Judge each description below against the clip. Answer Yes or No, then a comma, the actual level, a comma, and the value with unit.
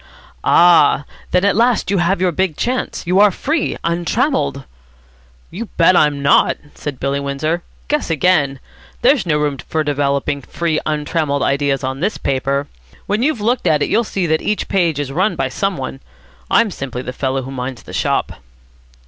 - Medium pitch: Yes, medium, 155 Hz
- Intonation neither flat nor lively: No, wide, 5.7 semitones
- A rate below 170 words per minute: No, average, 175 wpm